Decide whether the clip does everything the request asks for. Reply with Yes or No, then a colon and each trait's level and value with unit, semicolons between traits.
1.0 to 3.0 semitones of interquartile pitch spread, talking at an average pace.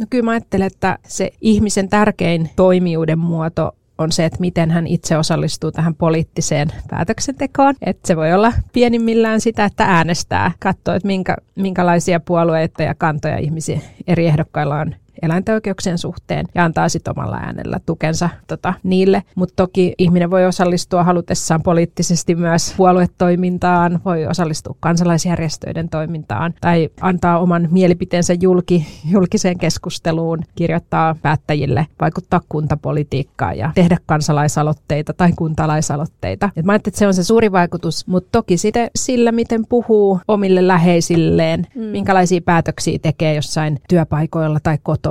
Yes: average, 2.7 semitones; average, 135 wpm